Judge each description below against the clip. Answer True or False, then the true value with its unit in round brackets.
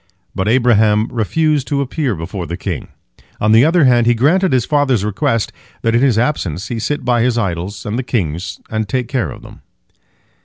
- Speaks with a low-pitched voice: True (115 Hz)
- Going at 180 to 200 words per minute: True (195 wpm)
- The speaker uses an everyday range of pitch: True (4.3 semitones)